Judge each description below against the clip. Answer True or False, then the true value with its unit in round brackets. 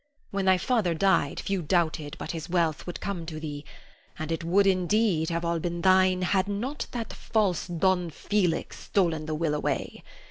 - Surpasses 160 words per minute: True (180 wpm)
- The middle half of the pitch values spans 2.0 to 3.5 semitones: True (3.1 semitones)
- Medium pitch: True (175 Hz)